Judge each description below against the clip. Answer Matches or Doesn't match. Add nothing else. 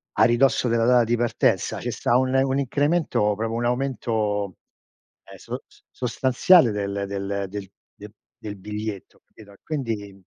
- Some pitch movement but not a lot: Matches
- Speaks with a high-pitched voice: Doesn't match